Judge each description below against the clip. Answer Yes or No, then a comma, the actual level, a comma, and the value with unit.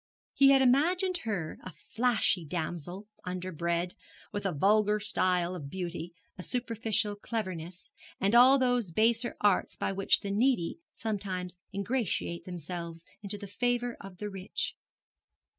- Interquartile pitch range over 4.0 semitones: Yes, average, 4.6 semitones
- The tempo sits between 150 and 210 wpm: No, slow, 135 wpm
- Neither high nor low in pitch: No, high, 200 Hz